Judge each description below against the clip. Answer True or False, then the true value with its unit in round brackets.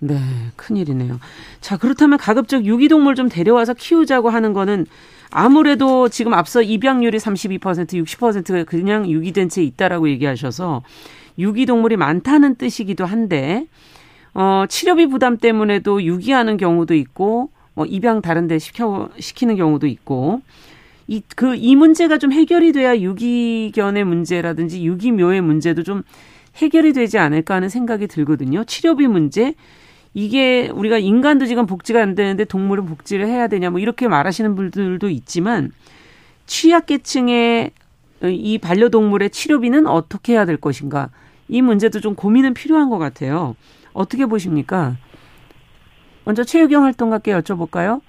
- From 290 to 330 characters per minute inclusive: True (325 characters per minute)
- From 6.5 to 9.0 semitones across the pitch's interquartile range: False (6.0 semitones)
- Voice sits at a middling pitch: False (210 Hz)